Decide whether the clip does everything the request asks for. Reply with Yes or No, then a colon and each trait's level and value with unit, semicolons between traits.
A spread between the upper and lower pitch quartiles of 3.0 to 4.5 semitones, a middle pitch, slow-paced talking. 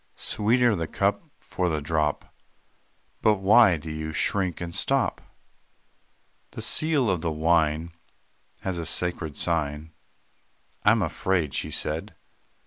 No: average, 4.1 semitones; very low, 85 Hz; slow, 130 wpm